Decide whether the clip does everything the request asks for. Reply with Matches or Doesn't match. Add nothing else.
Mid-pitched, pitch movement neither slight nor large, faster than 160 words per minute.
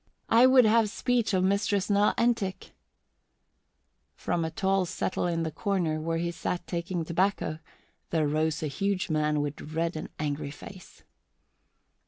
Doesn't match